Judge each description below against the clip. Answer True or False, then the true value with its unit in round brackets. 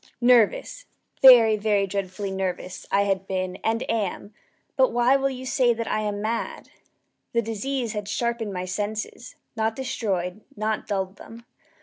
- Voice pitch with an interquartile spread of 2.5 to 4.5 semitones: True (3.2 semitones)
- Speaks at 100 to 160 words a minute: True (150 wpm)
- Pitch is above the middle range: True (215 Hz)